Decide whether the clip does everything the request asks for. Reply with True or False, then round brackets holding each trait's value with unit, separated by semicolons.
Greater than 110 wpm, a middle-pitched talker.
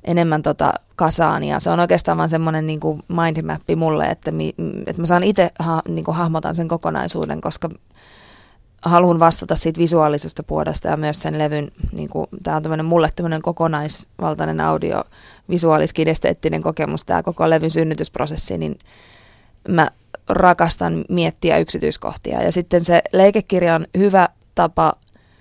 True (140 wpm; 160 Hz)